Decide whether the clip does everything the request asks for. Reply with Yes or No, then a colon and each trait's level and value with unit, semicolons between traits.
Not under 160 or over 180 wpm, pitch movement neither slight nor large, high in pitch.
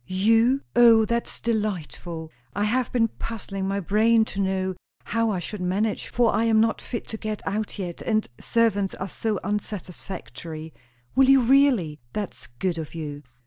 Yes: average, 165 wpm; average, 3.5 semitones; high, 210 Hz